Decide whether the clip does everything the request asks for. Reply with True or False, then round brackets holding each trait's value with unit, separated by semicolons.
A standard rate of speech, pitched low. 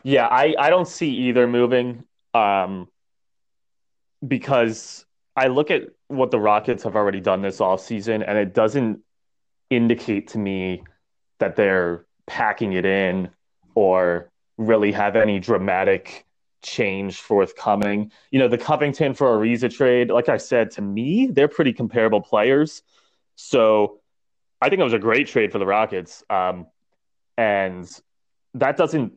True (145 wpm; 105 Hz)